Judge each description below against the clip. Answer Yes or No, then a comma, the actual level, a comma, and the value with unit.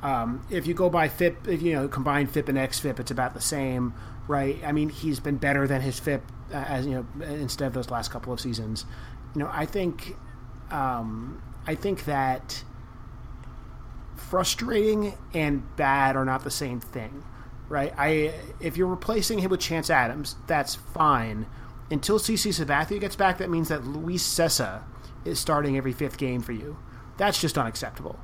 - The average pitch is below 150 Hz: Yes, medium, 140 Hz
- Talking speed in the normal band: Yes, average, 180 wpm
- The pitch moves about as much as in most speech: Yes, average, 4.5 semitones